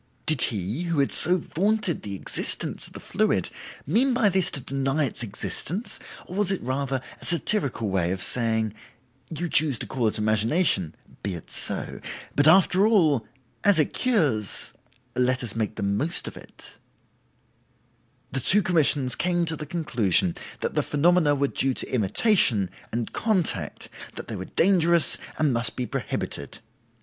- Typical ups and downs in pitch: No, wide, 7.5 semitones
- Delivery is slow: No, average, 160 wpm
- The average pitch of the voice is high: No, medium, 140 Hz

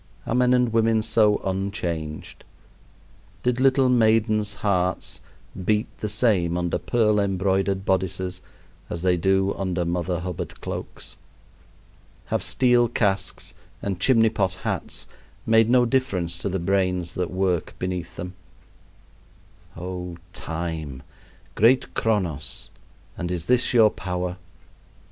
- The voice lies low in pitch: Yes, very low, 95 Hz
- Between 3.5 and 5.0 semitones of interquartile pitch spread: Yes, average, 3.9 semitones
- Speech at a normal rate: No, slow, 120 wpm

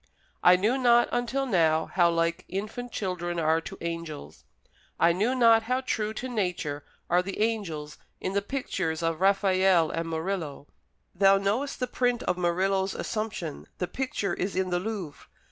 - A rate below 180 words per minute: Yes, average, 160 wpm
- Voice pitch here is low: No, high, 190 Hz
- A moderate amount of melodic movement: Yes, average, 4.8 semitones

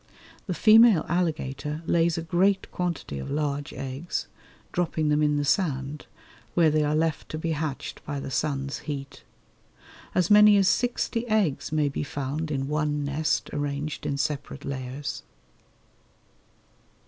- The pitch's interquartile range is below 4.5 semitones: Yes, average, 3.3 semitones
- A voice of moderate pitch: Yes, medium, 150 Hz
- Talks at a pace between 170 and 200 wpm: No, average, 145 wpm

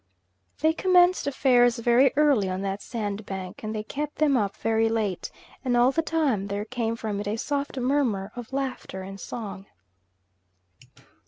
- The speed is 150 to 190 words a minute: Yes, average, 160 wpm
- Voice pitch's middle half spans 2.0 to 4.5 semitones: No, average, 5.1 semitones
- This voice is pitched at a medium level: No, high, 230 Hz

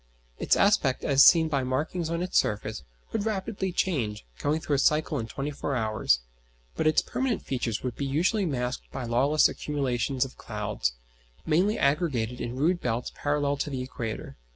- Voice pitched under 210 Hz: Yes, medium, 140 Hz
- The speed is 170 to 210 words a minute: Yes, average, 175 wpm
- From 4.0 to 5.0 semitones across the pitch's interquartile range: Yes, average, 4.7 semitones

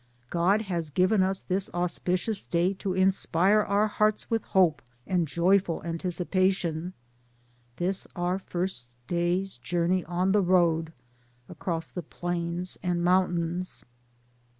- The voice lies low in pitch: No, medium, 180 Hz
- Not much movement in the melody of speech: Yes, narrow, 1.9 semitones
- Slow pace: Yes, slow, 125 wpm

